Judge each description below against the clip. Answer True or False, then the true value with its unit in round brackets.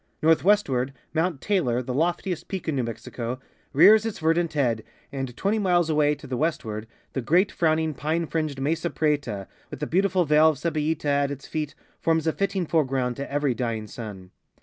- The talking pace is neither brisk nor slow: True (180 wpm)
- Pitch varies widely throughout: False (4.2 semitones)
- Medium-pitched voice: True (150 Hz)